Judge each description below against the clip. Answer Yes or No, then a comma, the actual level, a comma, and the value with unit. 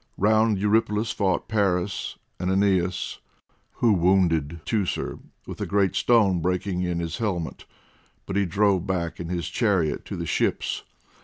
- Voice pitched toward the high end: No, very low, 95 Hz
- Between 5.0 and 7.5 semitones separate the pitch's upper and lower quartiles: No, average, 2.7 semitones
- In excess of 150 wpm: No, average, 145 wpm